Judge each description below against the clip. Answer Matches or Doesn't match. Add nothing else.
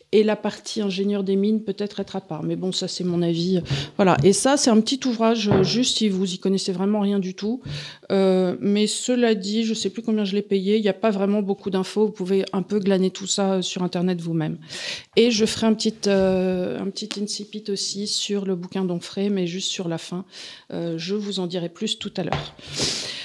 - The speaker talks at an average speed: Doesn't match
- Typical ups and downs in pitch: Doesn't match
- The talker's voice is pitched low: Doesn't match